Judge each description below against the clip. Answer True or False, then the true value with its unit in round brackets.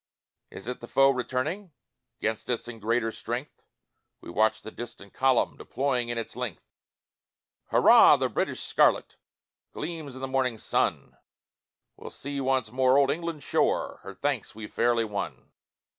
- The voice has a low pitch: True (125 Hz)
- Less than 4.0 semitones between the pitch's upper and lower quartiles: True (3.0 semitones)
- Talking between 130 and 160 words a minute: True (150 wpm)